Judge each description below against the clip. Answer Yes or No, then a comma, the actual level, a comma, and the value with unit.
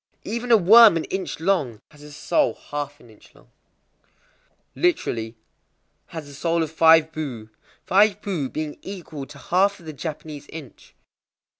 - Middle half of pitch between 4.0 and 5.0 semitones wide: Yes, average, 4.7 semitones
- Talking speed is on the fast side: No, average, 155 wpm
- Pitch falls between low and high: Yes, medium, 160 Hz